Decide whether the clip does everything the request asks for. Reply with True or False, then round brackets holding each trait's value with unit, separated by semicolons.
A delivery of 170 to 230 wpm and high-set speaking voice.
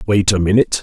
False (220 wpm; 100 Hz)